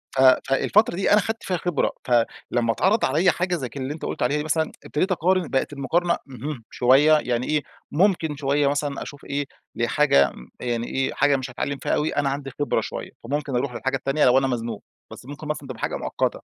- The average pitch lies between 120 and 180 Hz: Yes, medium, 140 Hz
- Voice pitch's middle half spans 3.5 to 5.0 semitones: No, average, 3.1 semitones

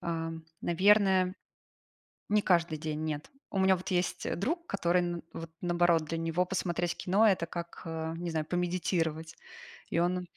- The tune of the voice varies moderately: No, narrow, 1.9 semitones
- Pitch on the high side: No, medium, 175 Hz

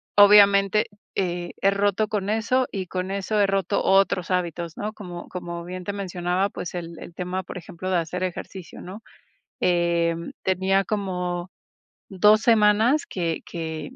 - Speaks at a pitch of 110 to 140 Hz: No, medium, 185 Hz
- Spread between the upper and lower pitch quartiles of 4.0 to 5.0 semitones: No, narrow, 2.5 semitones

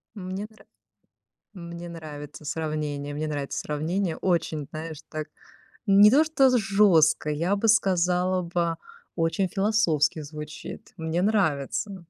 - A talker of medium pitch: Yes, medium, 170 Hz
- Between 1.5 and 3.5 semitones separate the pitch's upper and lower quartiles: No, average, 4.2 semitones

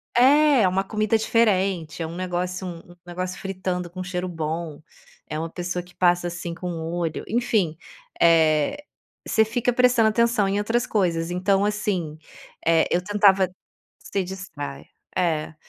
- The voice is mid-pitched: Yes, medium, 180 Hz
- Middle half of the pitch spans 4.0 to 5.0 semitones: No, average, 3.5 semitones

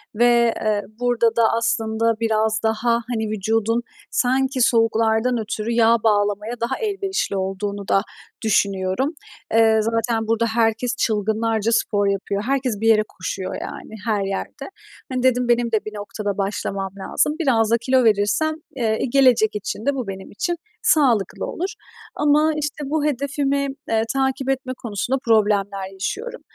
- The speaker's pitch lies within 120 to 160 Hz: No, high, 225 Hz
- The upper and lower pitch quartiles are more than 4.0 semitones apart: No, average, 3.4 semitones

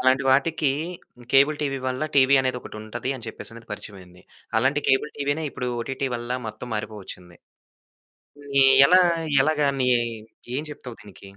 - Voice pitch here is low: Yes, low, 130 Hz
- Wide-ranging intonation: No, average, 3.9 semitones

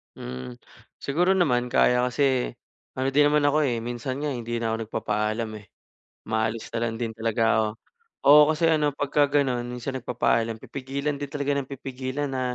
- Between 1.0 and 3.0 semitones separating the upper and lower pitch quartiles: No, average, 3.8 semitones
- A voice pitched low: Yes, low, 130 Hz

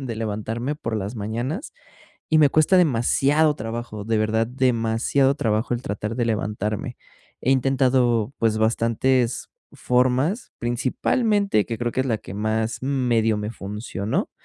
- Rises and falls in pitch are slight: No, average, 3.3 semitones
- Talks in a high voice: No, low, 120 Hz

